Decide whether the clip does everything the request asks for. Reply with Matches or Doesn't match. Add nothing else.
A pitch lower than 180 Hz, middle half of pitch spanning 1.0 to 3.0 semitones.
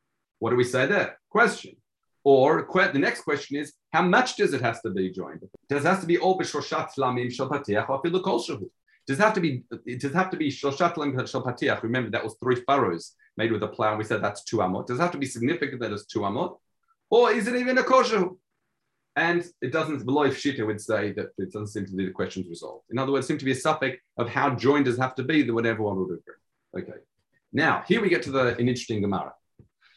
Doesn't match